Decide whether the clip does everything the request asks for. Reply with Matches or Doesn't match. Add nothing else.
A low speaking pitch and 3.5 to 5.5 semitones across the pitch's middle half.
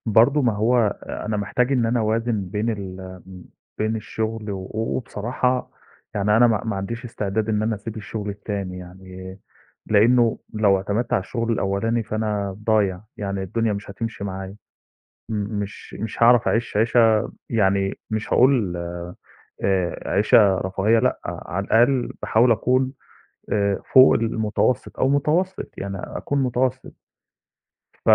Doesn't match